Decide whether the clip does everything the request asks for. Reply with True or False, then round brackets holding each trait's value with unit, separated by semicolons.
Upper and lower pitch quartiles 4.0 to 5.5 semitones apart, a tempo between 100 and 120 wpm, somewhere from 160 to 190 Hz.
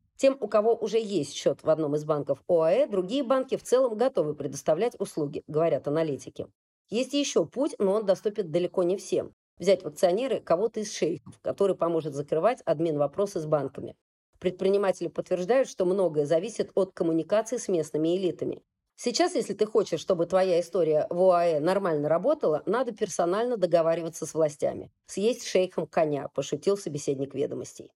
False (5.0 semitones; 160 wpm; 185 Hz)